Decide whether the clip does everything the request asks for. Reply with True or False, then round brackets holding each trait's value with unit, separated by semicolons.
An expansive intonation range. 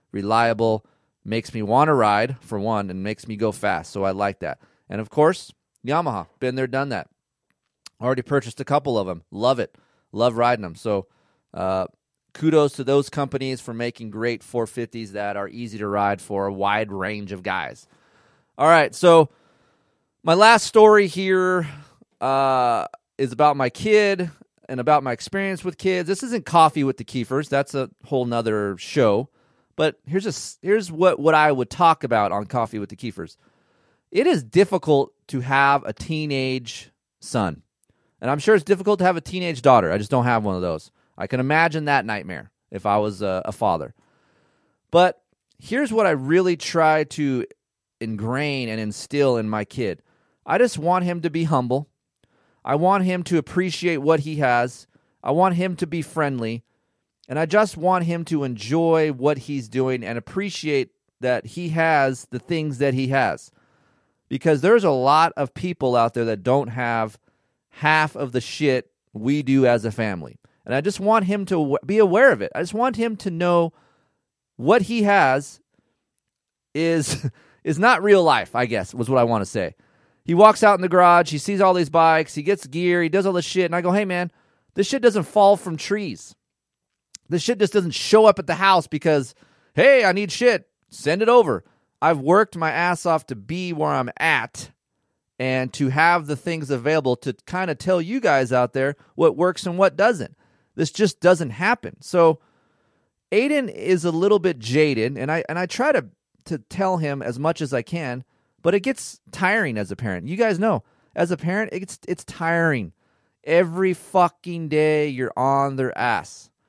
True (6.6 semitones)